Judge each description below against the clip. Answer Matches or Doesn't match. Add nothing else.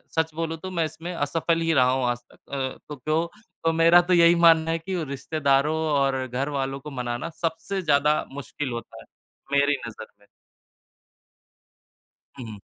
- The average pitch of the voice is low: Doesn't match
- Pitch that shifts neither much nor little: Matches